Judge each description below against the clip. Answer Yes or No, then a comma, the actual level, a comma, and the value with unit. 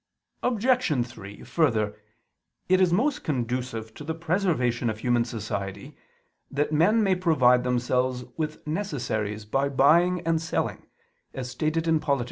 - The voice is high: No, medium, 140 Hz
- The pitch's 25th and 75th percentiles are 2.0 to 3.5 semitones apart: No, wide, 5.6 semitones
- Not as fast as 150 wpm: Yes, slow, 135 wpm